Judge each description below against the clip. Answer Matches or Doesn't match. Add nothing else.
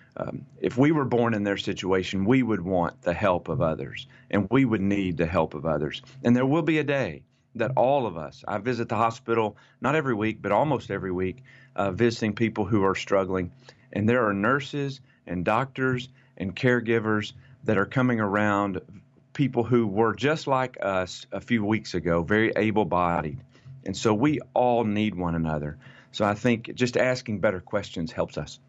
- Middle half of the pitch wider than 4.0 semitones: Matches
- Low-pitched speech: Matches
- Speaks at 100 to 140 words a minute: Doesn't match